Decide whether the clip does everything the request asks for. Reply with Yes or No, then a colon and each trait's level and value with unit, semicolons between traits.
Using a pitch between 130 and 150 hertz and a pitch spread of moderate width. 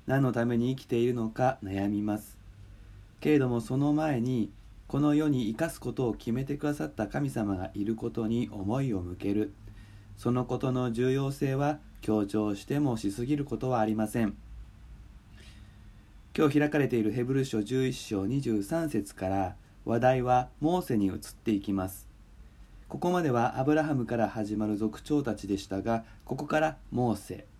No: low, 115 Hz; average, 4.2 semitones